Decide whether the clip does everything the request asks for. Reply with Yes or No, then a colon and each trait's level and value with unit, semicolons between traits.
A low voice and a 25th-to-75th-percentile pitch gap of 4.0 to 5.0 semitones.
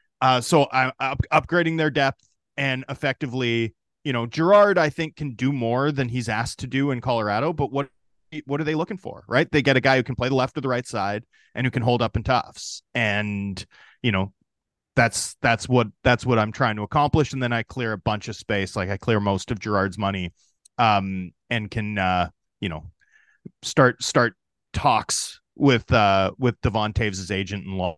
Yes: low, 125 Hz; average, 4.5 semitones